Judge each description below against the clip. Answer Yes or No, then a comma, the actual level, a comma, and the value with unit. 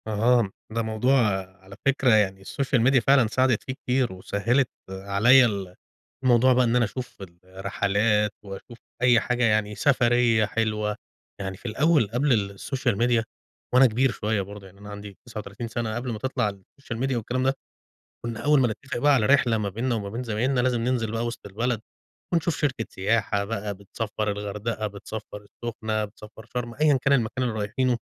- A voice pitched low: Yes, low, 115 Hz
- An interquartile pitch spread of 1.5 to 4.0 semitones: Yes, average, 3.4 semitones